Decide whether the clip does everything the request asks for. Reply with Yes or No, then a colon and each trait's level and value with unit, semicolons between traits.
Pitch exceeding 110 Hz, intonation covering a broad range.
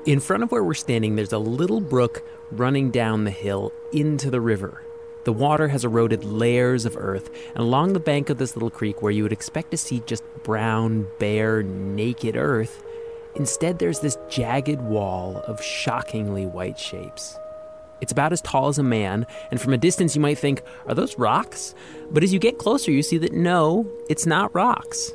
Yes: medium, 140 Hz; wide, 7.8 semitones